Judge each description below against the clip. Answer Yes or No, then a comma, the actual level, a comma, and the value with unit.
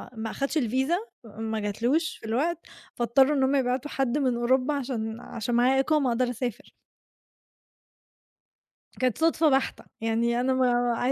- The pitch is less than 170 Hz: No, very high, 255 Hz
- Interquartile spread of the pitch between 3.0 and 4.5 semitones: No, narrow, 2.5 semitones